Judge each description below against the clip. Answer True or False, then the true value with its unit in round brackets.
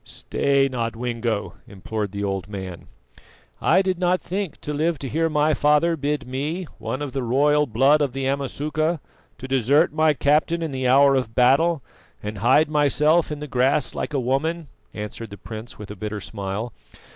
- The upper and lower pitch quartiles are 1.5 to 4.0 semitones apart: False (4.7 semitones)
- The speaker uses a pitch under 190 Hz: True (135 Hz)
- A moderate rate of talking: True (180 wpm)